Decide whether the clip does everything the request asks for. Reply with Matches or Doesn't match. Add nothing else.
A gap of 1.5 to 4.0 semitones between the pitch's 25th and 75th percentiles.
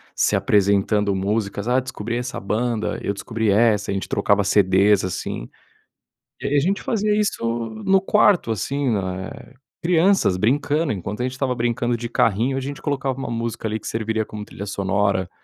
Doesn't match